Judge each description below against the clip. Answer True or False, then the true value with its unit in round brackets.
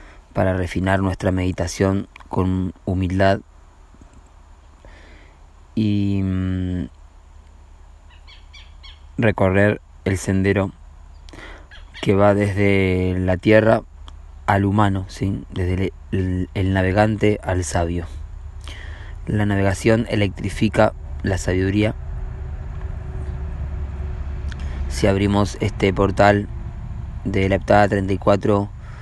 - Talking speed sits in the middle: False (80 wpm)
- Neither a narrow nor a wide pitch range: True (4.8 semitones)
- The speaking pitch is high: False (90 Hz)